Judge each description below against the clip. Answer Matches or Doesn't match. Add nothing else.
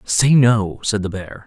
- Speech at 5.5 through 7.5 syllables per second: Doesn't match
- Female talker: Doesn't match